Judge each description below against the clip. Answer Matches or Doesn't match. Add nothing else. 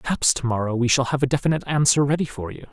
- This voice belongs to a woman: Doesn't match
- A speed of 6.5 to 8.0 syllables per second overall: Matches